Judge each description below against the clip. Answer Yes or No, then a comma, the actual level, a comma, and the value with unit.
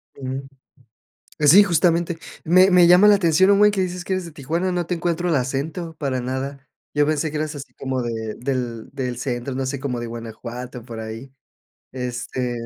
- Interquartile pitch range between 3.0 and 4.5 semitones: No, wide, 5.5 semitones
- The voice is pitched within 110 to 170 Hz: Yes, medium, 140 Hz